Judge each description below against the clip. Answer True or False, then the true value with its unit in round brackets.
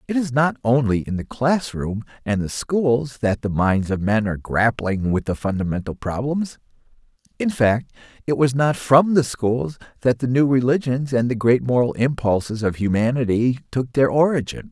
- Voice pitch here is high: False (125 Hz)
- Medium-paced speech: True (180 wpm)